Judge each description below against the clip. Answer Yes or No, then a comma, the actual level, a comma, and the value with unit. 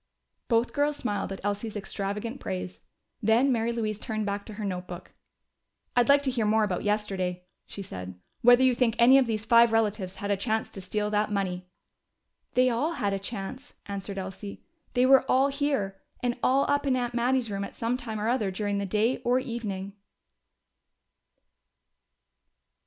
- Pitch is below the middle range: No, high, 215 Hz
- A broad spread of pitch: No, average, 3.7 semitones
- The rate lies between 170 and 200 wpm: Yes, average, 175 wpm